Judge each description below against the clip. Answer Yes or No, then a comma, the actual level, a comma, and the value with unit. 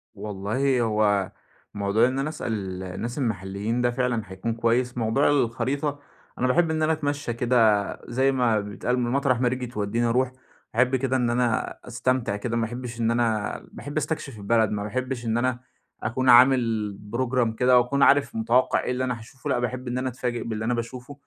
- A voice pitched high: No, low, 120 Hz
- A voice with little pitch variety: Yes, narrow, 2.3 semitones